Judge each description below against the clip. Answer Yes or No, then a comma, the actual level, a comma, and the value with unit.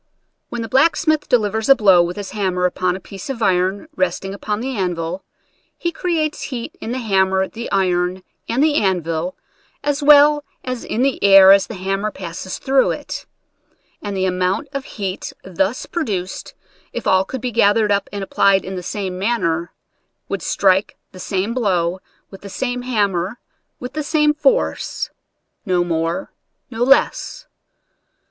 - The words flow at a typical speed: Yes, average, 165 wpm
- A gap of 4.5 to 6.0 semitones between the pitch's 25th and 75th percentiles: Yes, average, 5.3 semitones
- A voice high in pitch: Yes, high, 200 Hz